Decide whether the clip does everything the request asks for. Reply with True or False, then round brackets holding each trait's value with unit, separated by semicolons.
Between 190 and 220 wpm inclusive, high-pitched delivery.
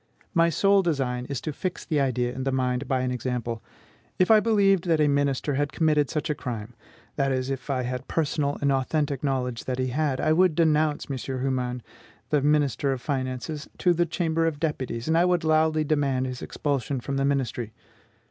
False (195 wpm; 140 Hz)